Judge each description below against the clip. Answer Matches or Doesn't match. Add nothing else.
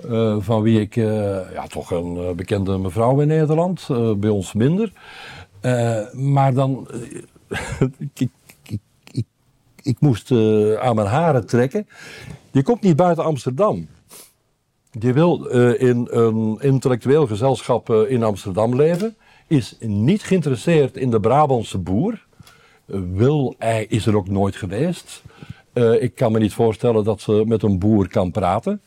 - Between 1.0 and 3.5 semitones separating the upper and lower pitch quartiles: Doesn't match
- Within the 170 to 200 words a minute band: Doesn't match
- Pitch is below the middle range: Matches